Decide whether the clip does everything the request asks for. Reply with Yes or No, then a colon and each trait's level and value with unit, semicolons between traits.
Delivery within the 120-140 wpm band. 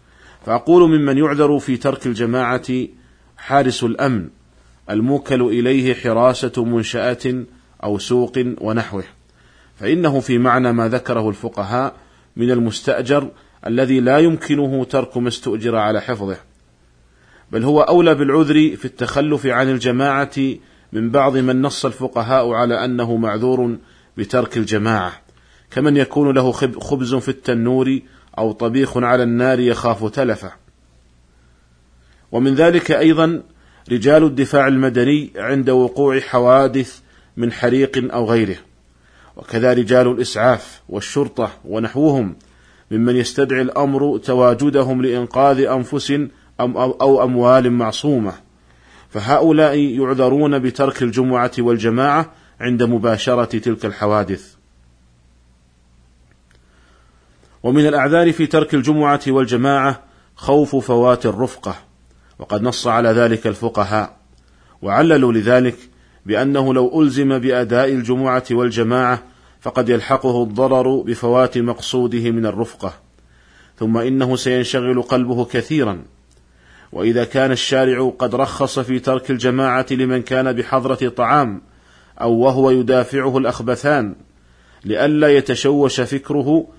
No: average, 105 wpm